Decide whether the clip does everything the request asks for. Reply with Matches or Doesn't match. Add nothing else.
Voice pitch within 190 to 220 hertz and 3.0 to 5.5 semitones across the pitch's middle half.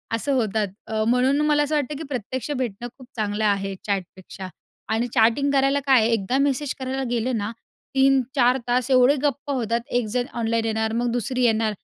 Doesn't match